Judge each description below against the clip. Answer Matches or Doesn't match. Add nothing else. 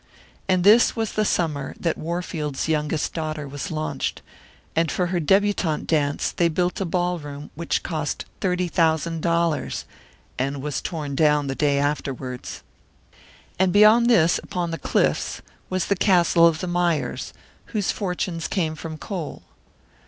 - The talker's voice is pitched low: Doesn't match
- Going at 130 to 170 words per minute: Matches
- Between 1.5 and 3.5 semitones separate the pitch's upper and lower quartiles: Matches